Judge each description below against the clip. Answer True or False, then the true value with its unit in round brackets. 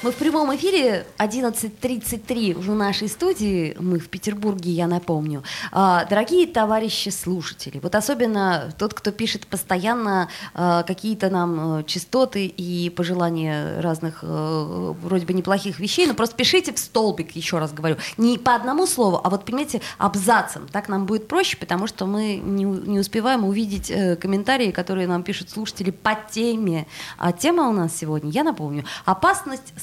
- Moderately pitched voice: False (195 Hz)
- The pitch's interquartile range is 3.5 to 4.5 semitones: True (4.2 semitones)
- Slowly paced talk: False (145 wpm)